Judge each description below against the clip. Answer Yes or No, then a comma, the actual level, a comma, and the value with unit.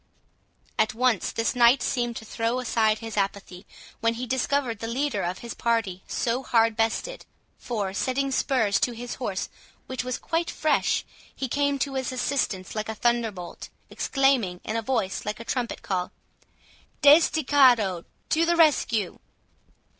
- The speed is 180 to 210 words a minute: No, average, 155 wpm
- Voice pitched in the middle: No, high, 235 Hz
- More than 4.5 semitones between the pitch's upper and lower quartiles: No, average, 3.6 semitones